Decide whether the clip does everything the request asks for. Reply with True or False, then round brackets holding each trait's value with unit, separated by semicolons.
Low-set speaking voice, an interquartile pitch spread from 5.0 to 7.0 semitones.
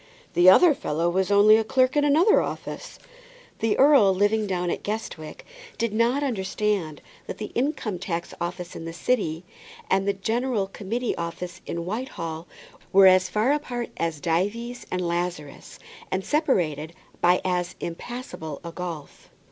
False (190 Hz; 5.3 semitones)